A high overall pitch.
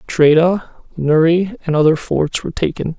No: medium, 165 Hz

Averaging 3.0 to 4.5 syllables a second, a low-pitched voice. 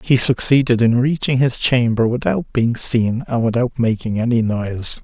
No: 4.7 syllables/s; low, 120 Hz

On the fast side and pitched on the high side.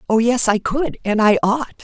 Yes: fast, 230 wpm; high, 235 Hz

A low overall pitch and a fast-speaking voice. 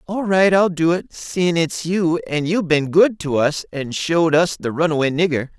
No: medium, 165 Hz; fast, 215 wpm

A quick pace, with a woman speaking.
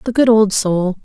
Yes: fast, 230 wpm; female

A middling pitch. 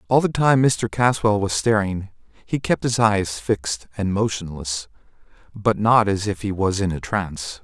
No: low, 100 Hz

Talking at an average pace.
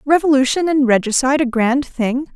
Yes: average, 155 wpm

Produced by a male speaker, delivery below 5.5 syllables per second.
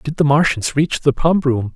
Yes: male; 5.1 syllables/s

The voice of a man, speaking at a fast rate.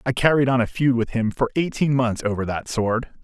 Yes: male; fast, 240 wpm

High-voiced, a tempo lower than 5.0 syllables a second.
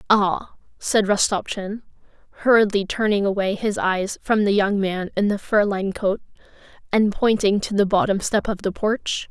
Yes: high, 205 Hz; 4.7 syllables/s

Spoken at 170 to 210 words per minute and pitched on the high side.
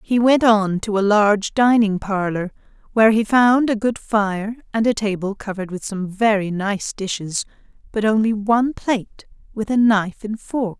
Yes: average, 180 wpm; high, 210 Hz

